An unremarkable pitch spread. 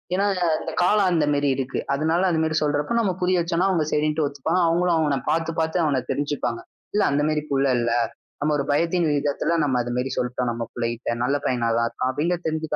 Yes: average, 3.9 semitones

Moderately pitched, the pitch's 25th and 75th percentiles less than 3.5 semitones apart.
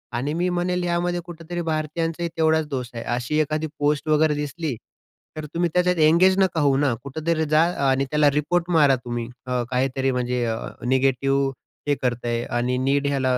No: medium, 150 Hz; average, 4.0 semitones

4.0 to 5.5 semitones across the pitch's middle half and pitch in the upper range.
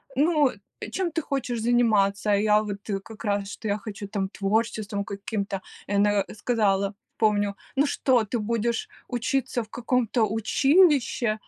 No: average, 3.2 semitones; high, 215 Hz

